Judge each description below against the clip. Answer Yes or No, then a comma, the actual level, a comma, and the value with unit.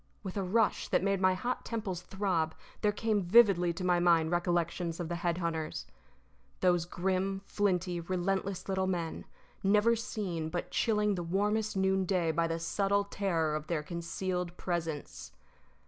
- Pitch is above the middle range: No, medium, 180 Hz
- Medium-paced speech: Yes, average, 155 wpm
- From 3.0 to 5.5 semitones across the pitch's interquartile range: No, narrow, 2.5 semitones